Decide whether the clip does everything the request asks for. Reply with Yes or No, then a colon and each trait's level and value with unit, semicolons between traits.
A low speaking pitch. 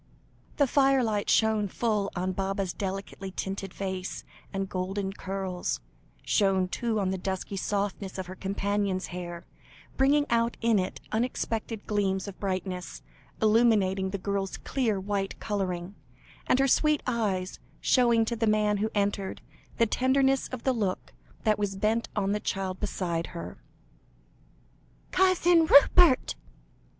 No: high, 200 Hz